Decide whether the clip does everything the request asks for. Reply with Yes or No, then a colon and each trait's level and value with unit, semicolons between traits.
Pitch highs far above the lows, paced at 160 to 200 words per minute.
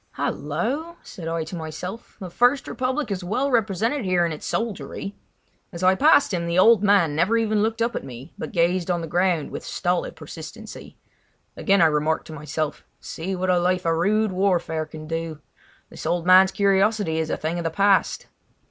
No: average, 4.4 semitones; average, 190 wpm